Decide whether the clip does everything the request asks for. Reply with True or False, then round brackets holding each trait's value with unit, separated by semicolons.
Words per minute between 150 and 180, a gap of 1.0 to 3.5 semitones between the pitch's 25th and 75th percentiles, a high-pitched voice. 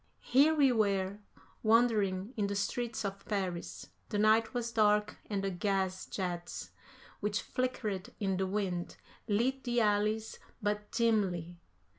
False (135 wpm; 2.8 semitones; 210 Hz)